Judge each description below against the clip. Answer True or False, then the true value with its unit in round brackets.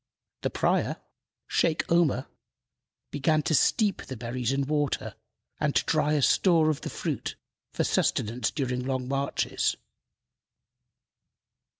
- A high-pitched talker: False (140 Hz)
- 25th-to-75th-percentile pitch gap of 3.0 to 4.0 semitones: True (3.4 semitones)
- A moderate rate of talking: False (120 wpm)